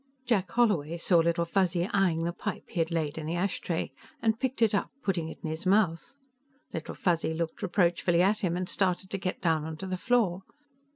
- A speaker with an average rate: No, fast, 210 wpm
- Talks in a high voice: No, medium, 175 Hz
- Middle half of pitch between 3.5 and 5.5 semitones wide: No, average, 2.9 semitones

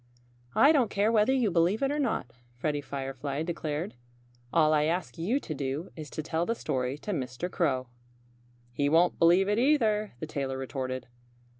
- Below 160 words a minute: No, average, 175 wpm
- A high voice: No, medium, 165 Hz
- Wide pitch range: Yes, wide, 6.9 semitones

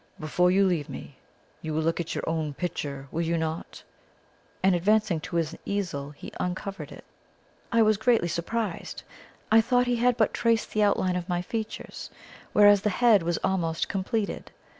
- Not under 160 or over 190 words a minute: Yes, average, 175 wpm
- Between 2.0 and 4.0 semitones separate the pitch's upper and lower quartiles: No, average, 4.5 semitones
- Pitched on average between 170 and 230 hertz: Yes, medium, 185 Hz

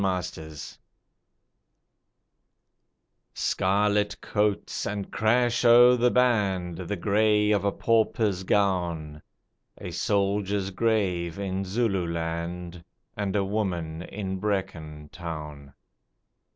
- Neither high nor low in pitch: No, very low, 95 Hz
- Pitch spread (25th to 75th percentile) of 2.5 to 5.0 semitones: Yes, average, 3.3 semitones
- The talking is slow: Yes, slow, 90 wpm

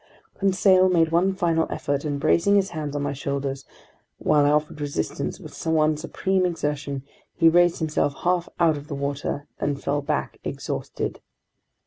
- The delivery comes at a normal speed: Yes, average, 160 wpm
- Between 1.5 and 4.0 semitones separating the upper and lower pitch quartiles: Yes, average, 3.4 semitones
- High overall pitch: No, medium, 155 Hz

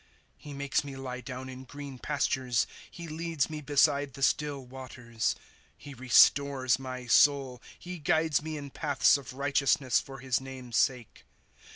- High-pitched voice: No, low, 135 Hz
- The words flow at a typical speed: Yes, average, 165 wpm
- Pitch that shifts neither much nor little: No, narrow, 2.0 semitones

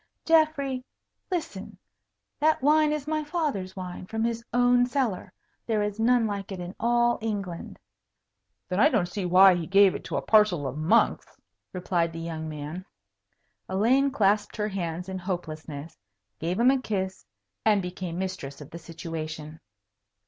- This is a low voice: No, high, 195 Hz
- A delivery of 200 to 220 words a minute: No, average, 155 wpm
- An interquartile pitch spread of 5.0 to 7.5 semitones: Yes, wide, 5.6 semitones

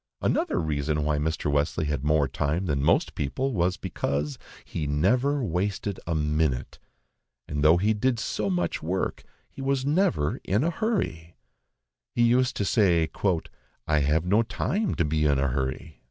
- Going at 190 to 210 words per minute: No, average, 165 wpm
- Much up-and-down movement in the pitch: Yes, wide, 6.7 semitones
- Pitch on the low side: Yes, very low, 80 Hz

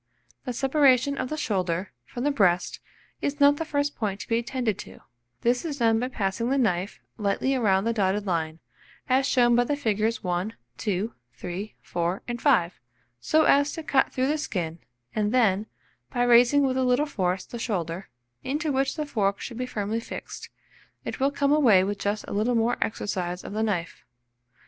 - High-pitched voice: Yes, high, 230 Hz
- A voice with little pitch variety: No, average, 5.3 semitones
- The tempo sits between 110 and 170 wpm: No, average, 185 wpm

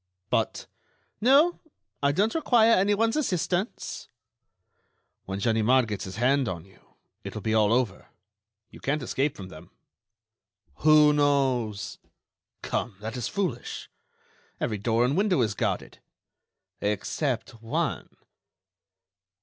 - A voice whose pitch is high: No, low, 130 Hz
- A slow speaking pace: Yes, slow, 115 wpm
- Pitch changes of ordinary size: No, wide, 8.8 semitones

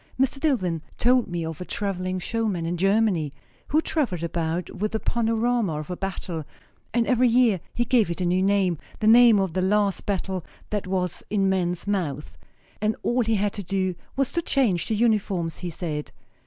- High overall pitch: Yes, high, 195 Hz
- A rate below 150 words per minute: No, average, 190 wpm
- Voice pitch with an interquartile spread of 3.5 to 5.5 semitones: Yes, average, 4.3 semitones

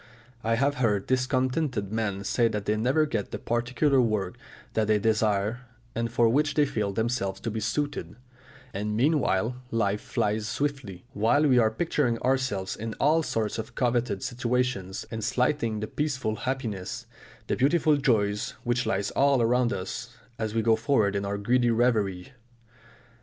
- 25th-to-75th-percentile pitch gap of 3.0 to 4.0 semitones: Yes, average, 3.4 semitones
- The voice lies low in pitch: Yes, low, 115 Hz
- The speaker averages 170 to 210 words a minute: No, average, 160 wpm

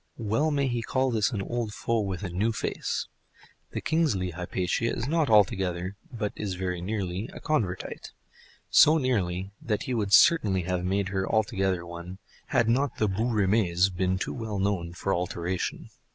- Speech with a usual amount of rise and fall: Yes, average, 4.1 semitones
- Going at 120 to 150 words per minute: No, average, 170 wpm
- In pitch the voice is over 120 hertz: No, low, 100 Hz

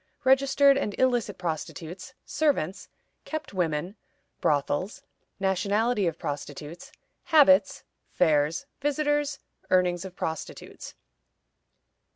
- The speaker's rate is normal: No, slow, 85 wpm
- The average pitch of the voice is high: Yes, high, 200 Hz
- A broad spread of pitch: Yes, wide, 8.7 semitones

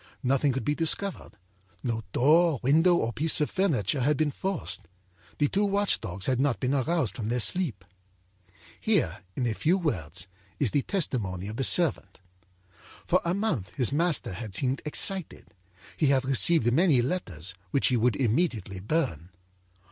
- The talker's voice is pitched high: No, low, 135 Hz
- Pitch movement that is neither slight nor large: No, wide, 7.0 semitones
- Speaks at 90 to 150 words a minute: No, average, 165 wpm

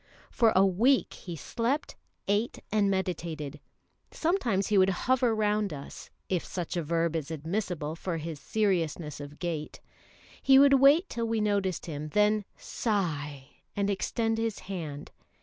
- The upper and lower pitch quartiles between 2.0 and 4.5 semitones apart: No, average, 5.3 semitones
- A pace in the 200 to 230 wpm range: No, average, 150 wpm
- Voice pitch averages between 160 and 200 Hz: Yes, high, 190 Hz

